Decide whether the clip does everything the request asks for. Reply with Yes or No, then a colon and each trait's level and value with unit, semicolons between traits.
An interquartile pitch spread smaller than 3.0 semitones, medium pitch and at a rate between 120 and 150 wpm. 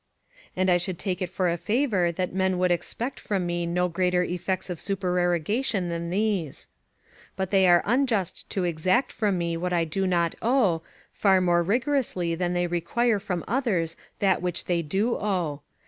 No: narrow, 2.6 semitones; medium, 180 Hz; average, 180 wpm